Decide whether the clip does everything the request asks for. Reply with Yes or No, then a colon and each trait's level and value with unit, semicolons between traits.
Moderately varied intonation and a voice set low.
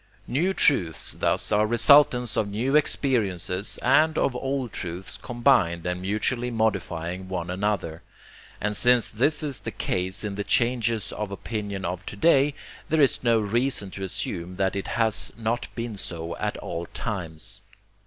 Yes: average, 4.9 semitones; low, 105 Hz